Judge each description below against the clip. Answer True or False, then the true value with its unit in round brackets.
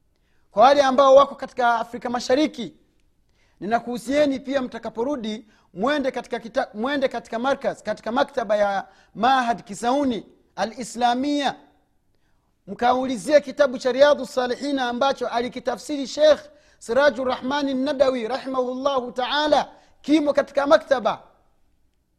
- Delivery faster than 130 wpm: False (105 wpm)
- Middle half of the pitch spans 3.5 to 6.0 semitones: False (2.9 semitones)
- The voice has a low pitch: False (255 Hz)